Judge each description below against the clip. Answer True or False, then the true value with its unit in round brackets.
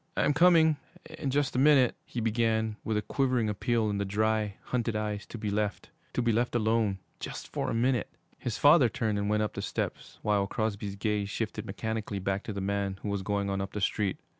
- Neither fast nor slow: False (215 wpm)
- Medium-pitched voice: False (110 Hz)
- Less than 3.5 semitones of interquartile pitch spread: True (2.8 semitones)